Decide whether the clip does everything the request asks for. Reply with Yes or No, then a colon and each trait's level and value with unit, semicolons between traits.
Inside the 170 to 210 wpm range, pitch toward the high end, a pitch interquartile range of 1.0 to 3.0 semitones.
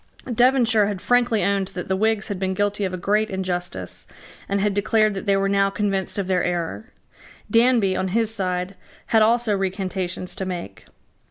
Yes: average, 180 wpm; high, 195 Hz; narrow, 2.6 semitones